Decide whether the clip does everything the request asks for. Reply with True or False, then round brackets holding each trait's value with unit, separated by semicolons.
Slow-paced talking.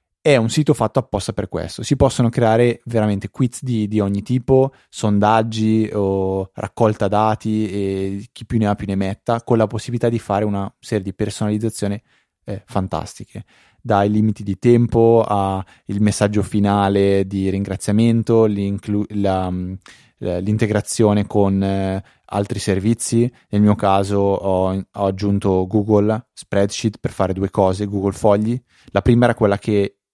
False (145 wpm)